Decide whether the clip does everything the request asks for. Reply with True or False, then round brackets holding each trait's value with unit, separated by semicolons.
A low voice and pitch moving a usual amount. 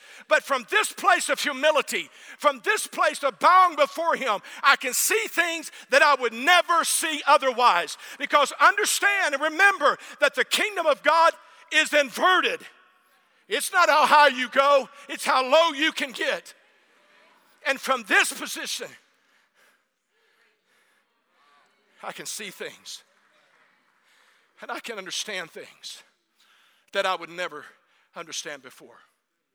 False (300 Hz; 3.7 semitones)